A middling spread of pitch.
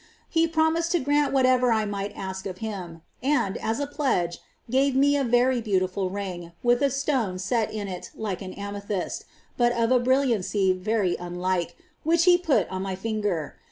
No: wide, 6.0 semitones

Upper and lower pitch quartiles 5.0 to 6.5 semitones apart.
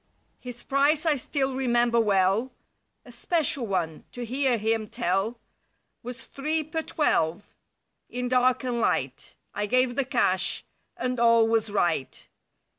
No: average, 3.4 semitones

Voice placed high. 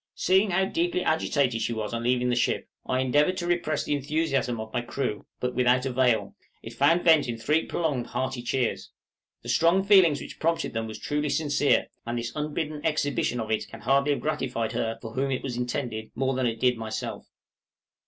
No: low, 130 Hz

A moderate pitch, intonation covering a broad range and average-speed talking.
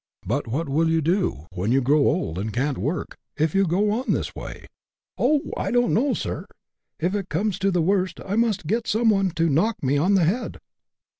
No: medium, 180 Hz; wide, 5.9 semitones; fast, 235 wpm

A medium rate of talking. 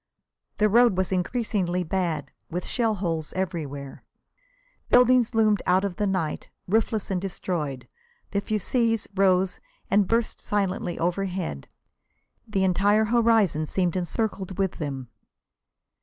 No: slow, 120 wpm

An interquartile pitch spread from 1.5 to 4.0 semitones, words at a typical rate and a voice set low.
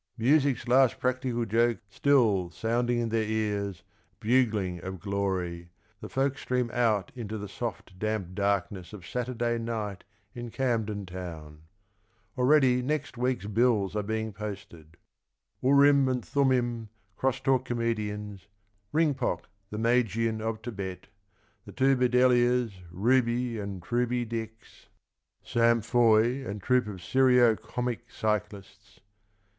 No: average, 3.5 semitones; slow, 125 wpm; low, 115 Hz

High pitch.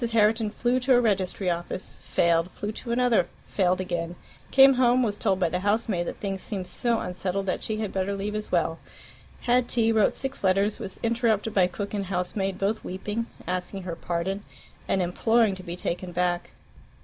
Yes: high, 195 Hz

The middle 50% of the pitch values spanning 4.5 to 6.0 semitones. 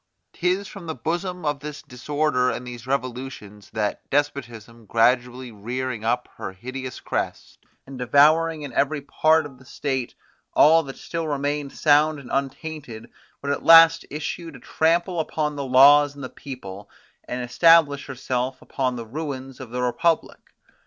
No: average, 3.6 semitones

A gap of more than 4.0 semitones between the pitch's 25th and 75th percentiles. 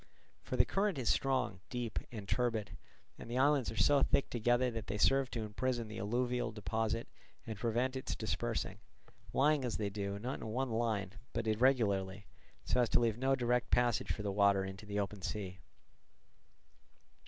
No: average, 3.4 semitones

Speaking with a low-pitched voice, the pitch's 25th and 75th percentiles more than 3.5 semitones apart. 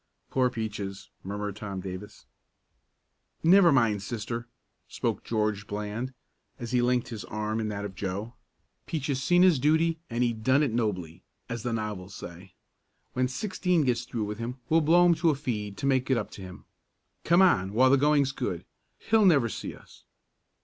Yes: low, 120 Hz; average, 5.2 semitones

